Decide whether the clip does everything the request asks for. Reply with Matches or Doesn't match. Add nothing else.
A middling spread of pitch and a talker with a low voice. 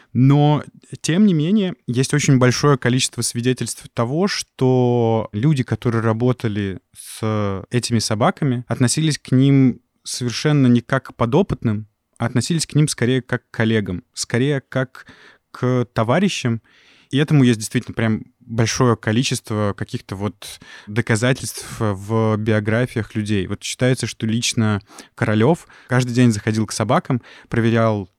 Matches